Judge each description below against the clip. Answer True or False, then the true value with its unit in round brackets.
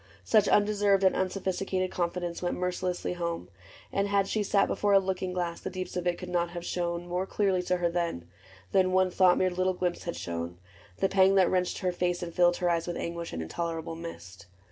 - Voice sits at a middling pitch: True (180 Hz)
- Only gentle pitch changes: True (1.6 semitones)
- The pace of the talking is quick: True (210 wpm)